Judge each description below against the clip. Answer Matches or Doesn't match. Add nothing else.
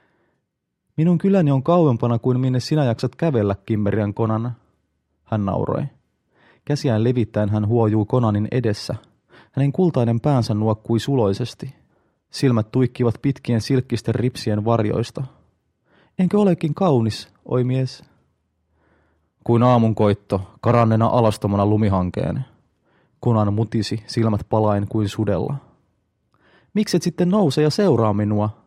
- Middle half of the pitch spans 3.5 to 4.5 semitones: Matches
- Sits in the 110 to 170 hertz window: Matches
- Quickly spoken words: Doesn't match